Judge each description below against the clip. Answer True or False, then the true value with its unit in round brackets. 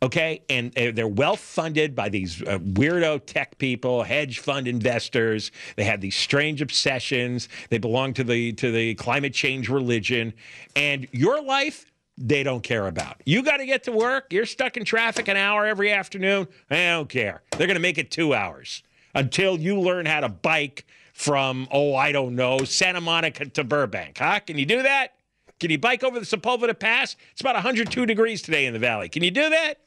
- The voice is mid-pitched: True (150 Hz)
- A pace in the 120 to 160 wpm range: False (195 wpm)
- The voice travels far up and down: True (8.4 semitones)